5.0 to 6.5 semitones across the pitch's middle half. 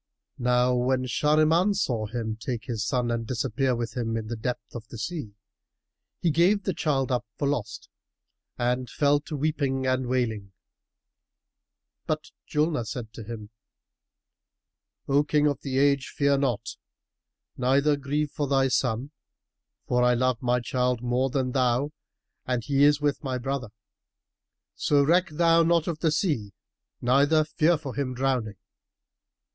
No: average, 3.3 semitones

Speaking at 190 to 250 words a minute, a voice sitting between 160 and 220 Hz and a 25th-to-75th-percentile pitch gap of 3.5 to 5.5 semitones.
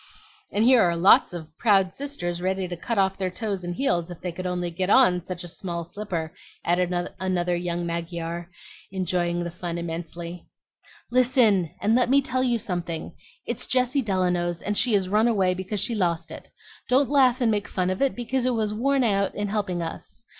Yes: average, 195 wpm; medium, 185 Hz; average, 4.4 semitones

